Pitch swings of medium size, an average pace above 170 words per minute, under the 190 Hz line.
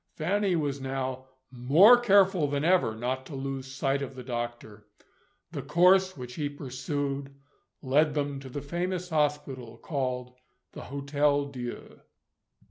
No: average, 3.0 semitones; slow, 135 wpm; medium, 140 Hz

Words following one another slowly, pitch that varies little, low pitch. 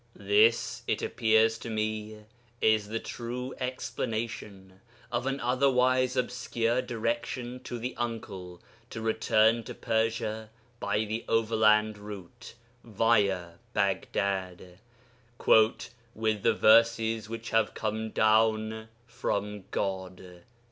Yes: slow, 105 wpm; narrow, 1.8 semitones; low, 110 Hz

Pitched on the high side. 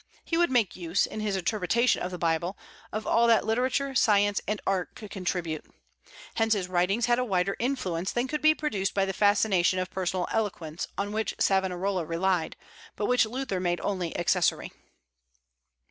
Yes: high, 195 Hz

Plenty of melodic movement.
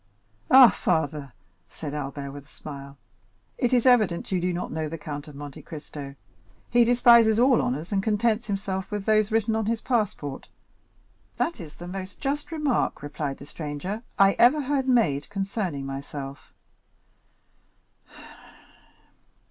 Yes: wide, 8.0 semitones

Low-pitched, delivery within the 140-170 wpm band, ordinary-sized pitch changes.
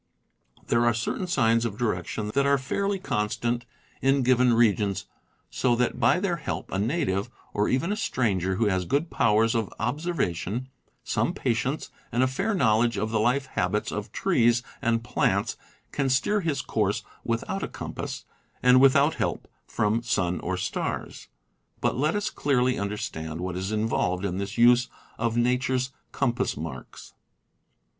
Yes: low, 120 Hz; average, 160 wpm; average, 4.2 semitones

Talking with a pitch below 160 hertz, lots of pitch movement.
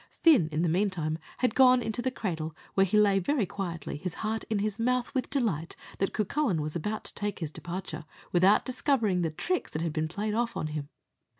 No: high, 195 Hz; wide, 5.9 semitones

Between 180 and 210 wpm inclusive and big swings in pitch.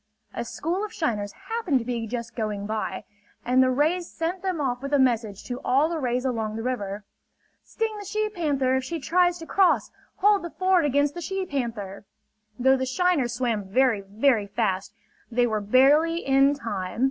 Yes: average, 190 wpm; wide, 6.6 semitones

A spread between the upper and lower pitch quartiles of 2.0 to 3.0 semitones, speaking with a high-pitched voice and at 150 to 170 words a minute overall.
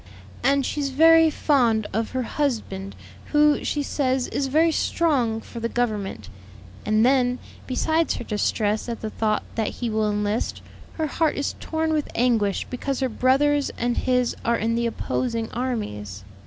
No: average, 4.3 semitones; high, 245 Hz; average, 160 wpm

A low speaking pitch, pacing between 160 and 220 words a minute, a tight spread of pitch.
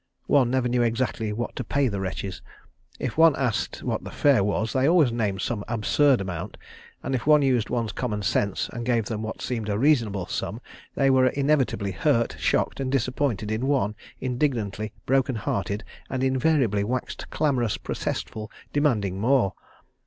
No: low, 120 Hz; average, 165 wpm; average, 4.2 semitones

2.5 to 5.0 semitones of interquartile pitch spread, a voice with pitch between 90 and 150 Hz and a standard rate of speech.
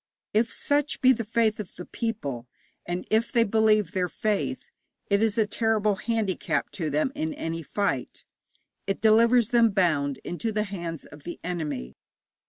No: average, 4.7 semitones; high, 205 Hz; average, 165 wpm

